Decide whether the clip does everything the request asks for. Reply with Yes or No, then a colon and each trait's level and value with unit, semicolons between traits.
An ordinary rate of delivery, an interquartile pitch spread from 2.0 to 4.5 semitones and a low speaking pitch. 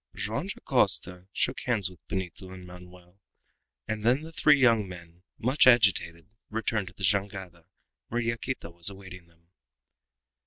Yes: average, 145 wpm; average, 4.1 semitones; very low, 95 Hz